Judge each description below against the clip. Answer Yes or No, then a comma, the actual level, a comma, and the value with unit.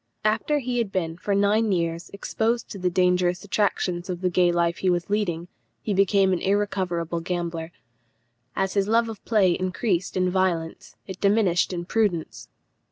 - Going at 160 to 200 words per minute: Yes, average, 165 wpm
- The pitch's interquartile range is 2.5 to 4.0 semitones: Yes, average, 2.9 semitones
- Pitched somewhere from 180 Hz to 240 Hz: Yes, medium, 185 Hz